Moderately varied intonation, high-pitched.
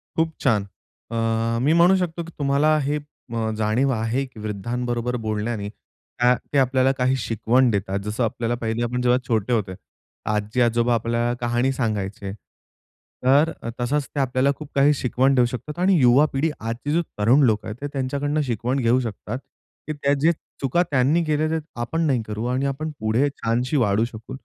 No: average, 3.7 semitones; low, 125 Hz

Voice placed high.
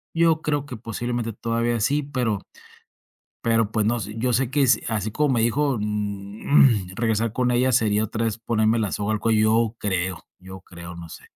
No: low, 115 Hz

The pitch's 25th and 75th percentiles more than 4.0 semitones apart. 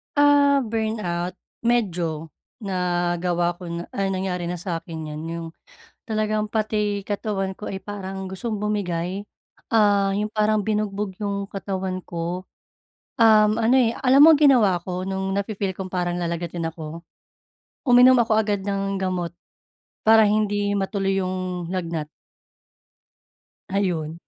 No: average, 3.2 semitones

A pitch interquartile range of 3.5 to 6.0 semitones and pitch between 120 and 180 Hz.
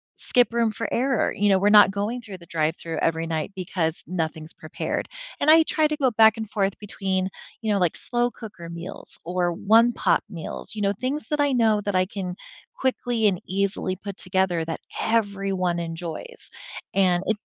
No: average, 4.2 semitones; high, 200 Hz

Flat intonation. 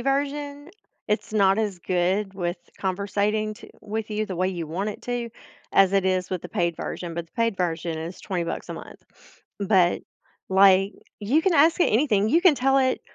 No: average, 4.5 semitones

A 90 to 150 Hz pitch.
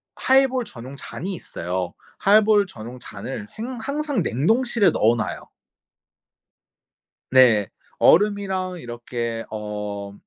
Yes: medium, 140 Hz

